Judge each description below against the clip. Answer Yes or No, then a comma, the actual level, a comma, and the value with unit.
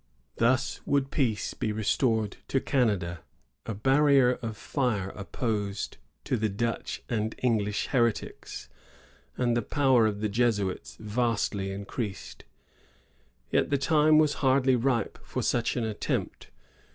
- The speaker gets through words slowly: Yes, slow, 125 wpm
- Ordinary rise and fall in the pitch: Yes, average, 3.9 semitones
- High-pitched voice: No, low, 115 Hz